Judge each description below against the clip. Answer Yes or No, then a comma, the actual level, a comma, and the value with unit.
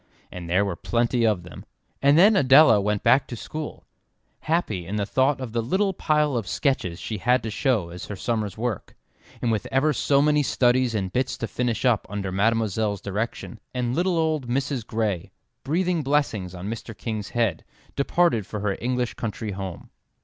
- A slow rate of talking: No, average, 185 wpm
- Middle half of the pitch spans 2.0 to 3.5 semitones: No, average, 5.0 semitones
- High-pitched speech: No, low, 115 Hz